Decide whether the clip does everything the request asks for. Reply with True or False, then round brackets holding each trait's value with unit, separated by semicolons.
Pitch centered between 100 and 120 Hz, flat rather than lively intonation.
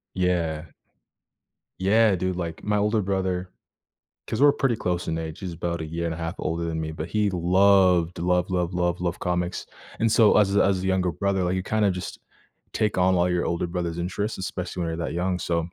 False (90 Hz; 2.1 semitones)